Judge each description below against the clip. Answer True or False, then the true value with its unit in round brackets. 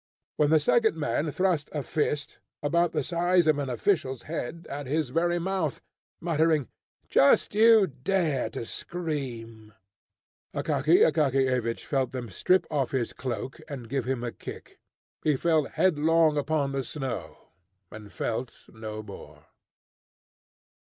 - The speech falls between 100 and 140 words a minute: True (135 wpm)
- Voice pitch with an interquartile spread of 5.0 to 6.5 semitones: False (4.3 semitones)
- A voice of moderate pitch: True (145 Hz)